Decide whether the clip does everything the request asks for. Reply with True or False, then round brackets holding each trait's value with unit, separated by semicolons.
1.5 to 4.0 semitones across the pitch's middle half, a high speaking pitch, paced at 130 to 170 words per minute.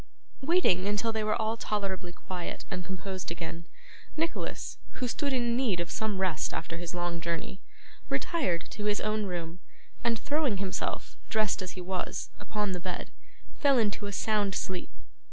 True (3.6 semitones; 195 Hz; 165 wpm)